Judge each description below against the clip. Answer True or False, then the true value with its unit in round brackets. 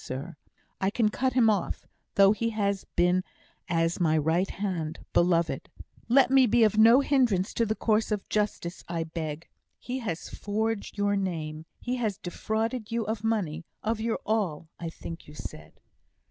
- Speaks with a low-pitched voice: False (205 Hz)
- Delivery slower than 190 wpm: True (165 wpm)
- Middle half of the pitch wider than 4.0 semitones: True (4.9 semitones)